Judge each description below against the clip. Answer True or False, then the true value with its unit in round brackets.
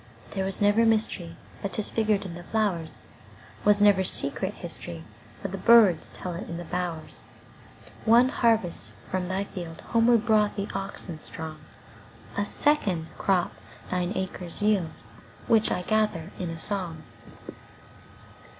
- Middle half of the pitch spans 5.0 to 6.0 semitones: False (3.7 semitones)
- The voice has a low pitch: False (195 Hz)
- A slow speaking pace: True (115 wpm)